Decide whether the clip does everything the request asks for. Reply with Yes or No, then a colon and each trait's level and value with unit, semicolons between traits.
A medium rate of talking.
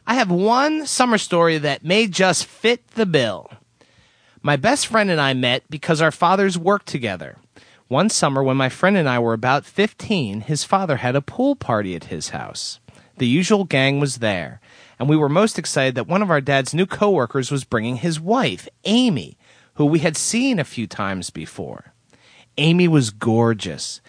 Yes: average, 185 wpm